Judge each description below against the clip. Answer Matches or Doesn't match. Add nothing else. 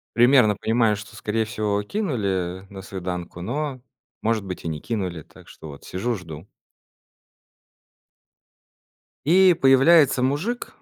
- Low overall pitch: Matches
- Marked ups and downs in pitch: Matches